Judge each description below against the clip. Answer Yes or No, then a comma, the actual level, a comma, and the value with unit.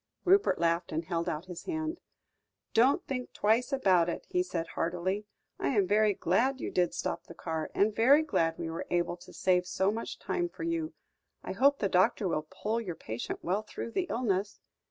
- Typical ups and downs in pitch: No, wide, 6.4 semitones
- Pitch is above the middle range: Yes, high, 195 Hz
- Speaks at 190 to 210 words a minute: Yes, average, 195 wpm